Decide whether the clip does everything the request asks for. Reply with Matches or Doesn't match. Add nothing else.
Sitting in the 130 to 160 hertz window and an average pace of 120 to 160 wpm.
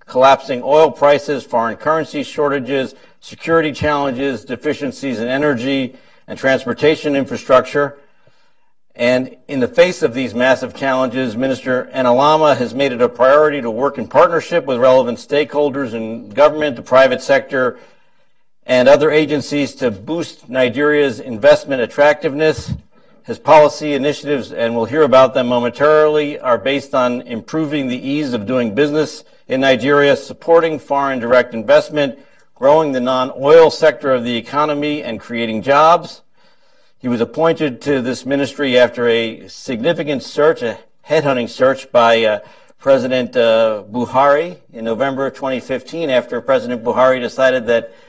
Matches